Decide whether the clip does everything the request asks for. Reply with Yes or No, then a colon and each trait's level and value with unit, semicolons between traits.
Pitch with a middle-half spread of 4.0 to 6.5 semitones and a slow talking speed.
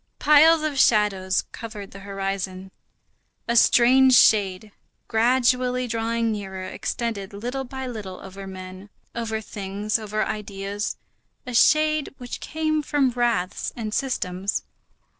Yes: average, 4.3 semitones; slow, 120 wpm